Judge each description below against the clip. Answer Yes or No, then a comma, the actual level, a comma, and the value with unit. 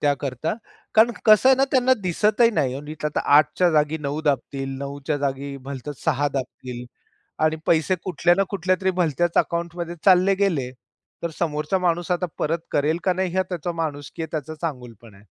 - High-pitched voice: No, medium, 160 Hz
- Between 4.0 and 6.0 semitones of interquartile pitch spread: Yes, average, 4.3 semitones